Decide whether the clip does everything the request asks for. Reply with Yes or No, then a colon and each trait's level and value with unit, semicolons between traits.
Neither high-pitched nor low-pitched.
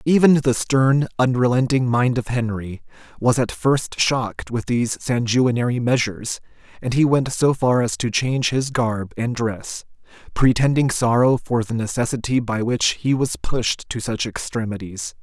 No: low, 120 Hz